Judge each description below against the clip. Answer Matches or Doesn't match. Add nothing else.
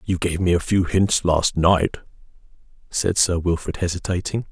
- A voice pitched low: Matches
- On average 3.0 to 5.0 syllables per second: Matches